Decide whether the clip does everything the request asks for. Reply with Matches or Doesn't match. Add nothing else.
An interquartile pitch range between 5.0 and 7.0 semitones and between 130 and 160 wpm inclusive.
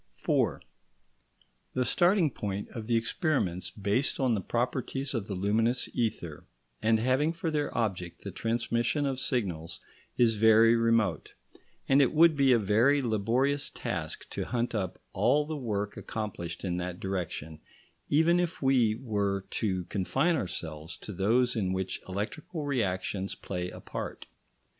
Matches